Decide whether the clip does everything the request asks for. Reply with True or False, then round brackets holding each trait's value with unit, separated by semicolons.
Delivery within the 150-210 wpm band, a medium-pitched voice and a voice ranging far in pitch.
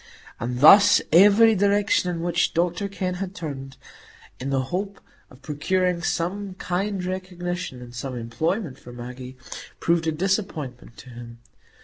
False (140 wpm; 170 Hz; 6.3 semitones)